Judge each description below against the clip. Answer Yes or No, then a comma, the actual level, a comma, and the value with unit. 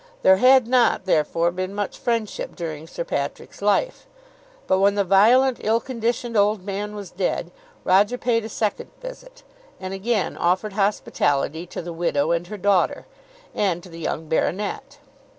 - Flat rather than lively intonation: No, average, 4.6 semitones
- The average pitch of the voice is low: No, high, 200 Hz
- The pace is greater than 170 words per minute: No, average, 160 wpm